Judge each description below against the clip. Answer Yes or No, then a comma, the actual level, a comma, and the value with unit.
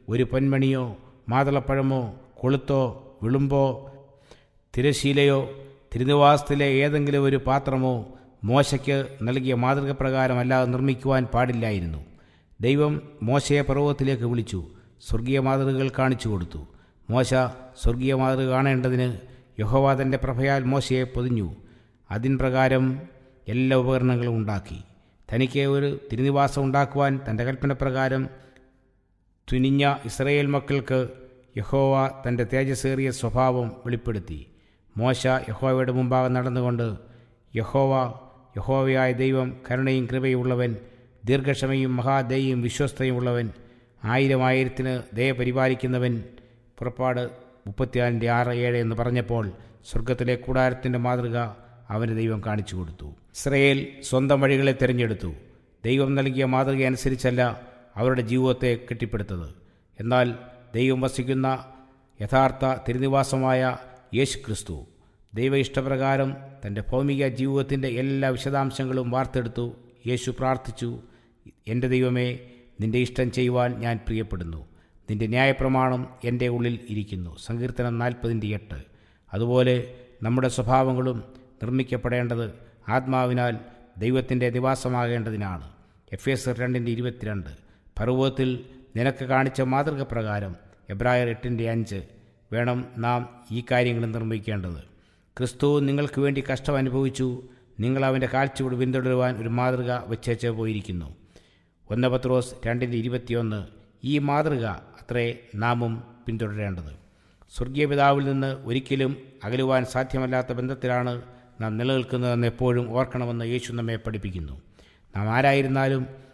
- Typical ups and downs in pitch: No, narrow, 2.2 semitones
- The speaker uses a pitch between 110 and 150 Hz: Yes, low, 125 Hz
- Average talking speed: No, slow, 95 wpm